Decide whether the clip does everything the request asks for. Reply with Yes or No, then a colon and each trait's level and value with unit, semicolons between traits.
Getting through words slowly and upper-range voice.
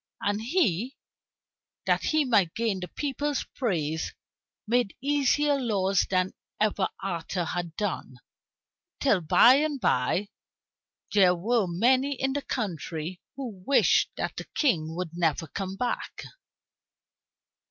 Yes: slow, 120 wpm; high, 205 Hz